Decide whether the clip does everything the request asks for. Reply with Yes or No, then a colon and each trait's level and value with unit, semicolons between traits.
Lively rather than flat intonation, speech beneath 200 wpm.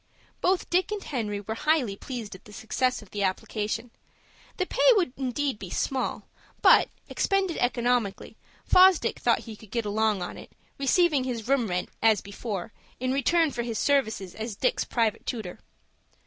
No: average, 4.9 semitones; average, 165 wpm